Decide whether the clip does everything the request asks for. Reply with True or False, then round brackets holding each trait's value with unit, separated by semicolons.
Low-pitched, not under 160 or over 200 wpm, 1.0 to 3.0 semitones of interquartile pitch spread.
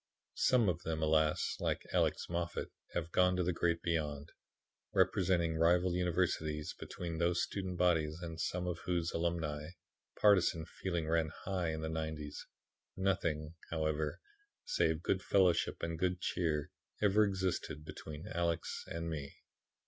False (85 Hz; 140 wpm; 2.4 semitones)